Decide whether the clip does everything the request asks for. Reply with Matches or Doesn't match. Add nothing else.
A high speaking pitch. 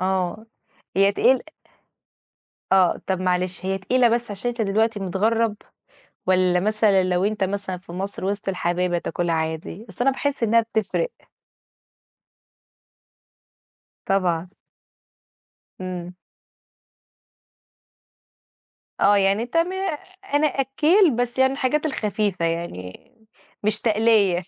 Matches